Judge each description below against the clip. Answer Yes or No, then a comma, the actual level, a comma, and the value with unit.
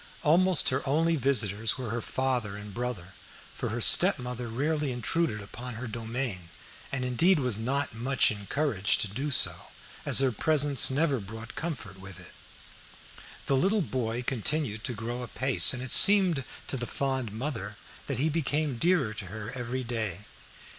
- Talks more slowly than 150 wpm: No, average, 160 wpm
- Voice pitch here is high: No, low, 125 Hz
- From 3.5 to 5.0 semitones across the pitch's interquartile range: Yes, average, 4.2 semitones